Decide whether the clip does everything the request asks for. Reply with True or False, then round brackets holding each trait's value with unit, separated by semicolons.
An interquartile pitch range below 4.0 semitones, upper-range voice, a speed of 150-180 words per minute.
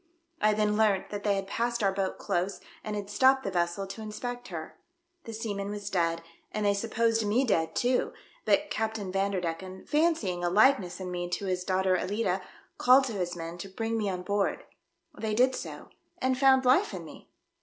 False (3.4 semitones; 205 Hz; 195 wpm)